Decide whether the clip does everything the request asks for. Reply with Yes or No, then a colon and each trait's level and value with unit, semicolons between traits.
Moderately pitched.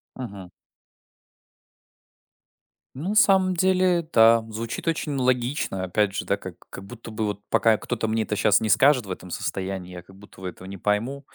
No: low, 110 Hz